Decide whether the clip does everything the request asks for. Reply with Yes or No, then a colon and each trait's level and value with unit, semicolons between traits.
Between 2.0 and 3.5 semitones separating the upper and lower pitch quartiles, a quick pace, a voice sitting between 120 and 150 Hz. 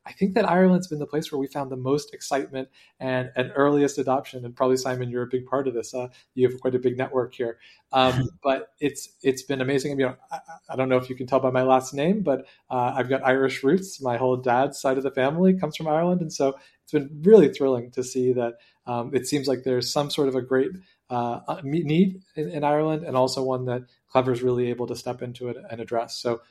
Yes: narrow, 2.4 semitones; fast, 250 wpm; low, 130 Hz